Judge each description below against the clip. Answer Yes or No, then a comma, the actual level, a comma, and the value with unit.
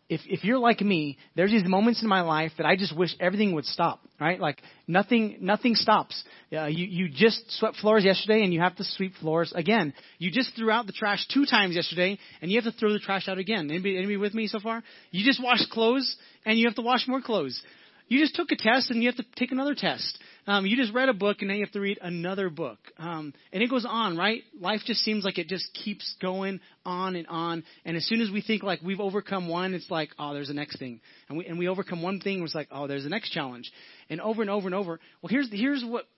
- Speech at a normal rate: No, fast, 260 wpm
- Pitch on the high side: Yes, high, 195 Hz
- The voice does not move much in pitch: No, average, 4.5 semitones